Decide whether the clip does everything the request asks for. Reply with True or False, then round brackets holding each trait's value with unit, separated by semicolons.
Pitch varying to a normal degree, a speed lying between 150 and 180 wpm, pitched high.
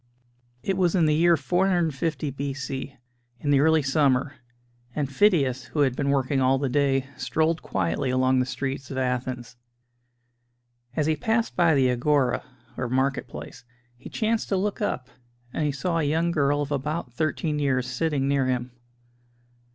False (3.5 semitones; 165 wpm; 140 Hz)